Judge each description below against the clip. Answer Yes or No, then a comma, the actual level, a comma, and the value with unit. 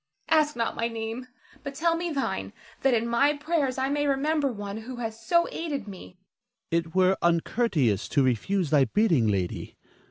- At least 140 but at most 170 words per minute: No, average, 180 wpm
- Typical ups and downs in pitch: No, wide, 7.5 semitones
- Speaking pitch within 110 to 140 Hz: No, high, 230 Hz